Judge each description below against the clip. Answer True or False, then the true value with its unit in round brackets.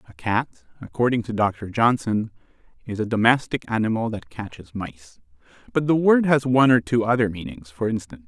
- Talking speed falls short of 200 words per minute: True (175 wpm)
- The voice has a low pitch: True (115 Hz)